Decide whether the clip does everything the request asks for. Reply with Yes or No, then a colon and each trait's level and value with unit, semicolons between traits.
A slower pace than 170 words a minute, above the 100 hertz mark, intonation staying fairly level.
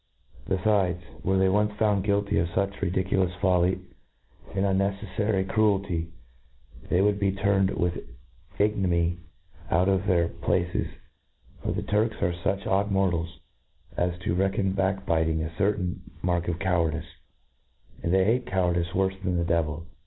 No: average, 160 wpm; very low, 95 Hz; narrow, 2.2 semitones